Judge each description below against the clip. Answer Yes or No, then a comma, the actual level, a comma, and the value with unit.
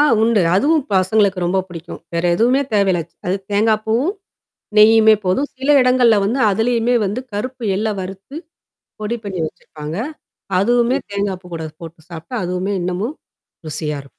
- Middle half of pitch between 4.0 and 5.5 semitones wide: Yes, average, 4.6 semitones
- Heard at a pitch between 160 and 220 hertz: Yes, high, 205 Hz